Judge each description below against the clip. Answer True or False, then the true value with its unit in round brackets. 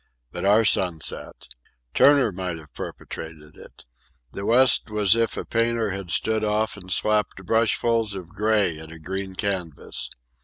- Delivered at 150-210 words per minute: True (155 wpm)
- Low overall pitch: True (100 Hz)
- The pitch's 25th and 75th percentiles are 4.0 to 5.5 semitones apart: False (3.6 semitones)